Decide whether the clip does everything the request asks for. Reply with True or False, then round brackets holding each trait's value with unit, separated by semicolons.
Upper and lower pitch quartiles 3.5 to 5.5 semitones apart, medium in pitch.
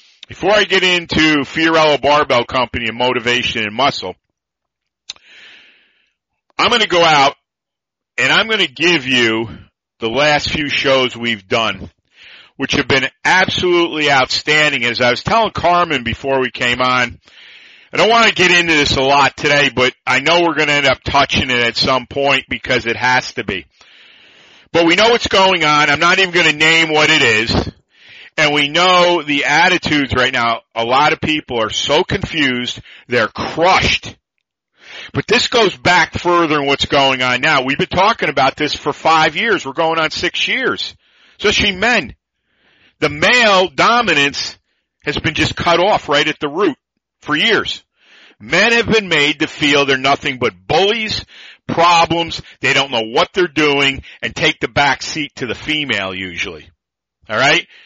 True (4.9 semitones; 145 Hz)